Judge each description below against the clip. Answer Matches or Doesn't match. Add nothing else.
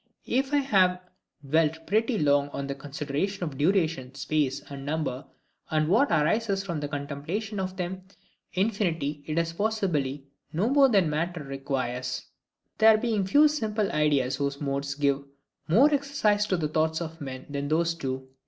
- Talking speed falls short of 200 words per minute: Matches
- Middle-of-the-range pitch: Matches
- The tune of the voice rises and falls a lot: Matches